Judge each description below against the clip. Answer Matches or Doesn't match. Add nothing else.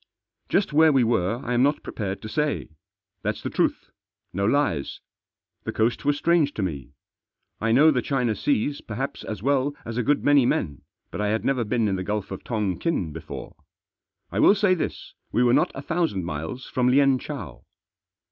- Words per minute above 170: Matches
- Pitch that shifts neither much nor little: Doesn't match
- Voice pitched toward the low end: Matches